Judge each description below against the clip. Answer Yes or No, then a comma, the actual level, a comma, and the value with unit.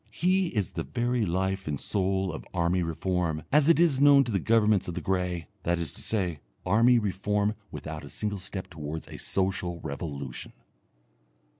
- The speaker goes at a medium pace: Yes, average, 175 wpm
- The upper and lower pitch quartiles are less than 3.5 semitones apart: No, average, 4.3 semitones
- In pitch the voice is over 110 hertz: No, very low, 95 Hz